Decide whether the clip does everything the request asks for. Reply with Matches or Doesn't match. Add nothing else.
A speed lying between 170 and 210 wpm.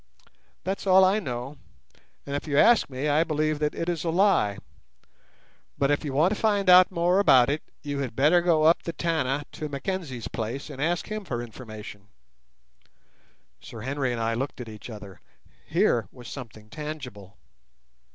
Matches